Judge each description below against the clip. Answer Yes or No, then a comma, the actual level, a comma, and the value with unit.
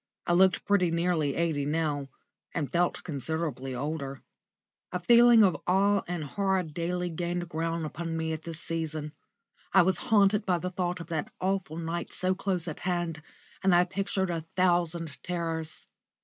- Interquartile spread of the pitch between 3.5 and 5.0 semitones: No, narrow, 2.4 semitones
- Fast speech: No, average, 165 wpm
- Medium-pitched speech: Yes, medium, 170 Hz